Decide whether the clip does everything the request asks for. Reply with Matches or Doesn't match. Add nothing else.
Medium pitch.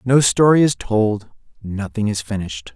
Doesn't match